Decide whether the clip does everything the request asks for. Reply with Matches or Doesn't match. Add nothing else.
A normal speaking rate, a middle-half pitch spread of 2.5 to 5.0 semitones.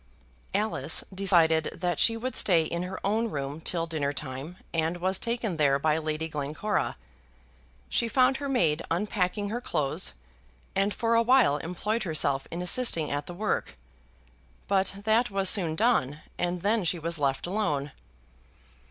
Doesn't match